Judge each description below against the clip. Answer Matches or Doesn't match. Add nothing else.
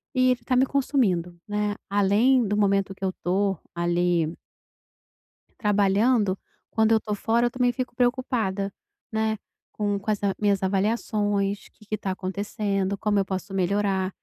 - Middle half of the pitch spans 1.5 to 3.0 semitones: Matches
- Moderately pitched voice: Doesn't match